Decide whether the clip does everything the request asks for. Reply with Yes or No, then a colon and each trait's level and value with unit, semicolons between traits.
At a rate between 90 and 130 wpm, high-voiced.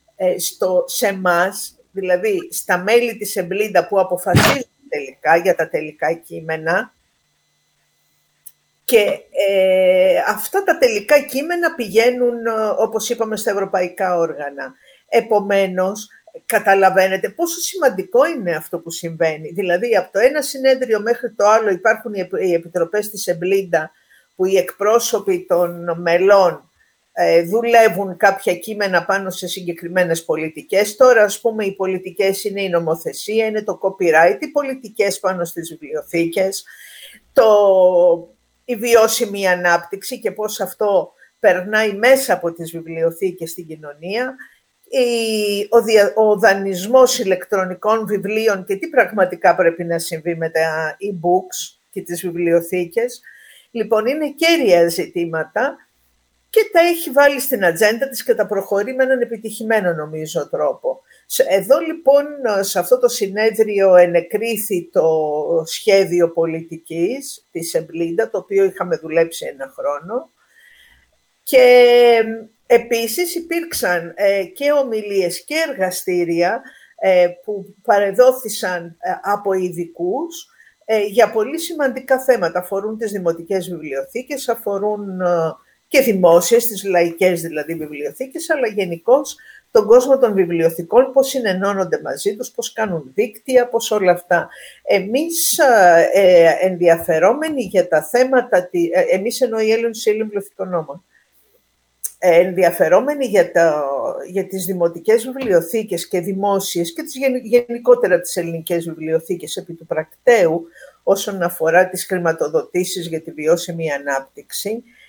Yes: average, 125 wpm; high, 195 Hz